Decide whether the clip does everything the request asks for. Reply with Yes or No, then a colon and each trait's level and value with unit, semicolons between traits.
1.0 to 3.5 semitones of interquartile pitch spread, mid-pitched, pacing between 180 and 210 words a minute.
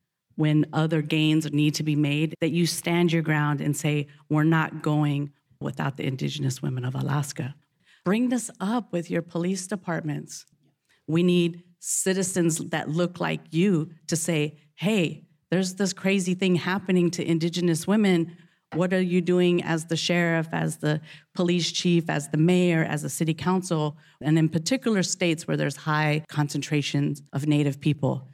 No: average, 2.8 semitones; medium, 160 Hz; average, 165 wpm